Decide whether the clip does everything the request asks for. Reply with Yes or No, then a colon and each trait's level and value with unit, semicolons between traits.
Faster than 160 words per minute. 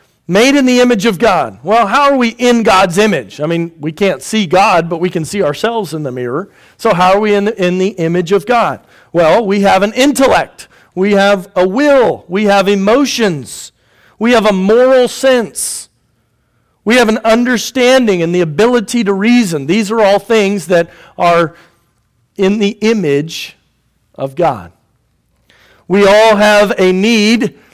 Yes: average, 175 wpm